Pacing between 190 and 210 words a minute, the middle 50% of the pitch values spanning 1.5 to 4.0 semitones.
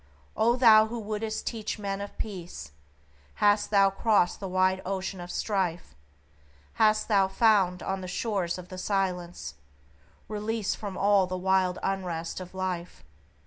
No: average, 145 wpm; narrow, 2.6 semitones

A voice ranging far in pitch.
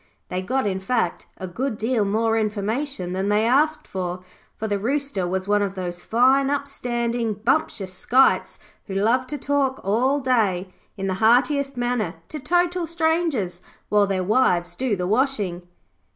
Yes: wide, 5.8 semitones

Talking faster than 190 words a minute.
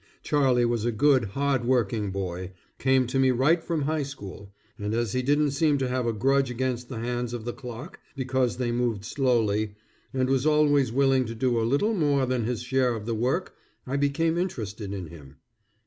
Yes: average, 200 wpm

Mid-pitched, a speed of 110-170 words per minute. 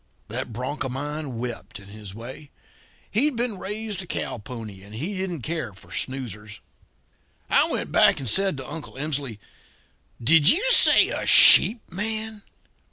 Yes: medium, 145 Hz; average, 160 wpm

